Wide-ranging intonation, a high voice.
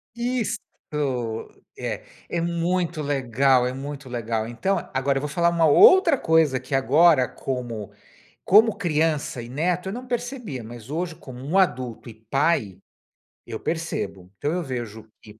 No: wide, 5.7 semitones; medium, 145 Hz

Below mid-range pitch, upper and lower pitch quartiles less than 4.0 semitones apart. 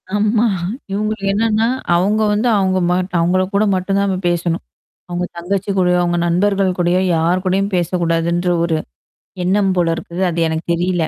No: medium, 185 Hz; narrow, 2.5 semitones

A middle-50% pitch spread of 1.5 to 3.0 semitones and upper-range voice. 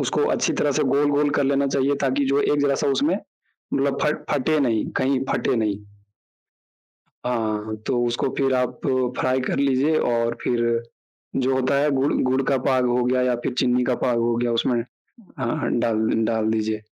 No: average, 2.7 semitones; low, 130 Hz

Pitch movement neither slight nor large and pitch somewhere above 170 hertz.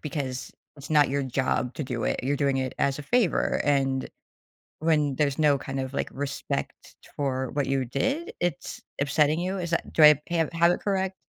No: average, 3.5 semitones; medium, 145 Hz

